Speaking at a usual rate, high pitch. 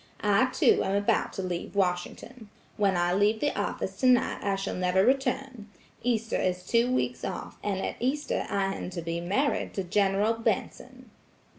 Yes: average, 170 wpm; high, 205 Hz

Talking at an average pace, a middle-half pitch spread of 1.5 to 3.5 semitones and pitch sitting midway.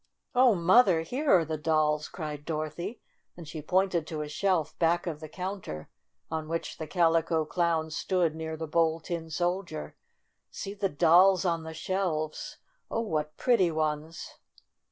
Yes: average, 160 wpm; average, 2.9 semitones; medium, 165 Hz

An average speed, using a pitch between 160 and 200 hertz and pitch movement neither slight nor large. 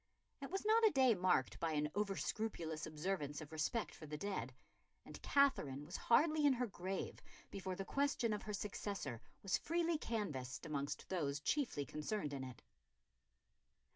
No: average, 165 wpm; high, 190 Hz; wide, 7.8 semitones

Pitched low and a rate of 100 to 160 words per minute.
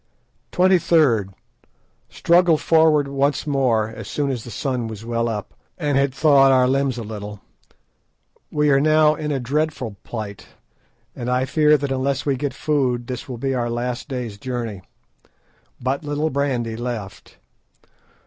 Yes: low, 130 Hz; average, 150 wpm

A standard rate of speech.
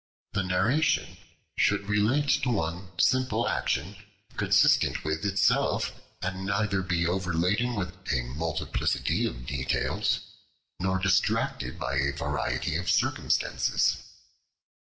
No: slow, 110 wpm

